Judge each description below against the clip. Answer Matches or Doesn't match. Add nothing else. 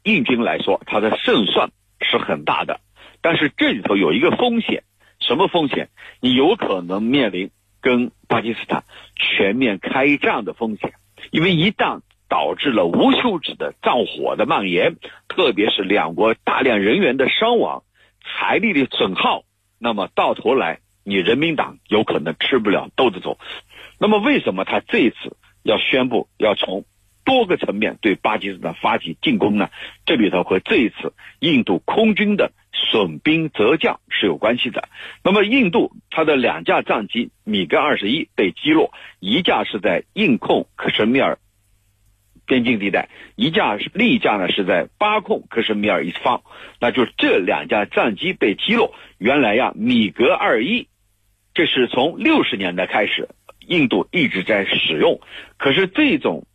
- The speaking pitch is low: Matches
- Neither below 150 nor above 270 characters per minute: Matches